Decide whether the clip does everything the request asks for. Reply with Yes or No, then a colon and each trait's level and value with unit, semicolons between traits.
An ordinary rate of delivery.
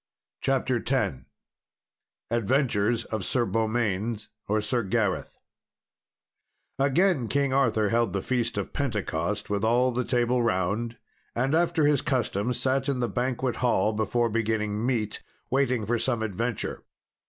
No: slow, 130 wpm